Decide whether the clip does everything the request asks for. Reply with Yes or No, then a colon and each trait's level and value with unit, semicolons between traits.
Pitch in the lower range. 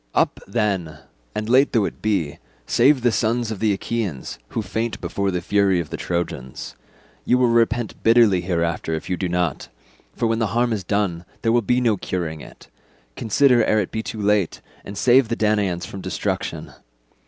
Yes: low, 105 Hz